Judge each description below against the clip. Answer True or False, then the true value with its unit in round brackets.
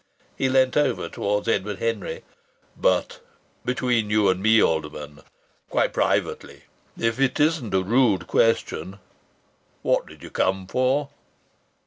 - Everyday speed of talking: False (125 wpm)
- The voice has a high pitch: False (110 Hz)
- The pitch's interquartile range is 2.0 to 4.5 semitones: False (5.1 semitones)